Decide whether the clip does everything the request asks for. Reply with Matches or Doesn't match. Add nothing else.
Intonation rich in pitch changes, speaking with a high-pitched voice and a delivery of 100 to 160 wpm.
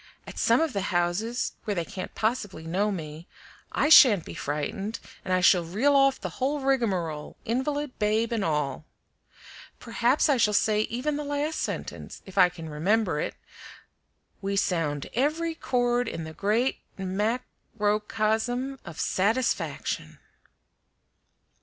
Matches